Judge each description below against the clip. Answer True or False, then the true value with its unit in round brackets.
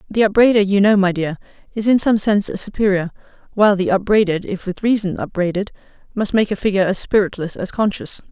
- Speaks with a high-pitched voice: True (200 Hz)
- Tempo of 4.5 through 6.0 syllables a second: False (6.3 syllables/s)